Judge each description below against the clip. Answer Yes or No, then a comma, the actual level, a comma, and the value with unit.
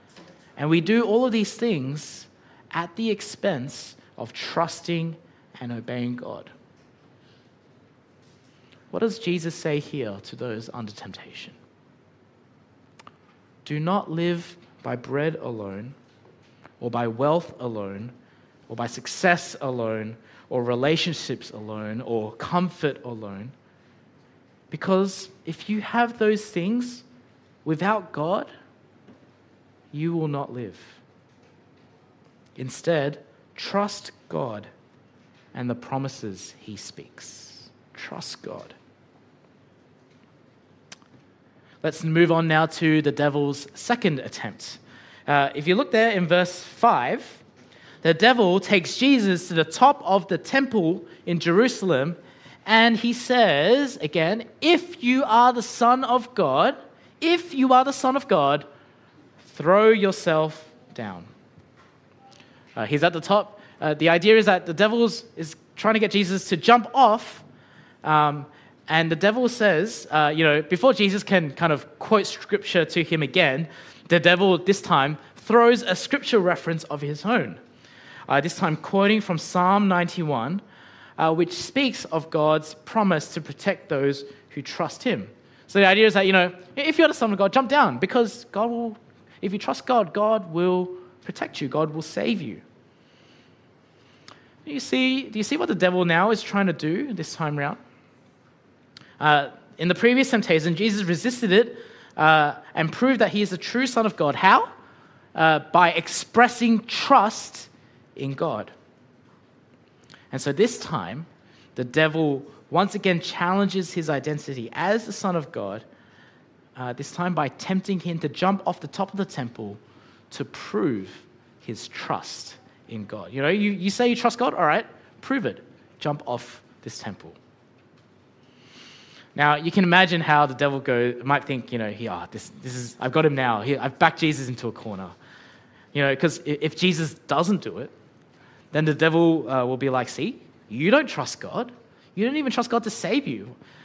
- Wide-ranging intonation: Yes, wide, 6.5 semitones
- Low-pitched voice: No, medium, 170 Hz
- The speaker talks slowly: No, average, 150 wpm